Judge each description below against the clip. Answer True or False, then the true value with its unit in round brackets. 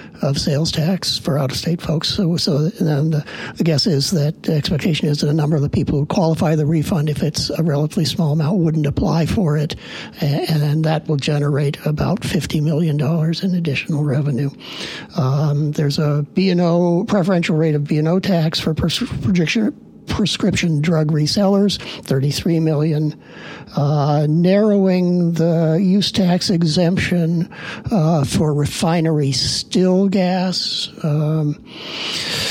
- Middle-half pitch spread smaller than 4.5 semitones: True (2.9 semitones)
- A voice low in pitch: False (160 Hz)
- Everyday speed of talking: True (150 wpm)